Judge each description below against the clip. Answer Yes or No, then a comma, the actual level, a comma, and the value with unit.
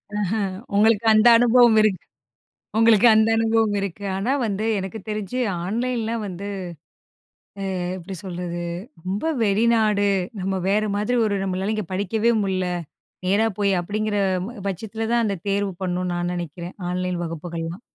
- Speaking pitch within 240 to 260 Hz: No, high, 205 Hz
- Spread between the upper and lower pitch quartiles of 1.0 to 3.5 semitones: Yes, average, 3.2 semitones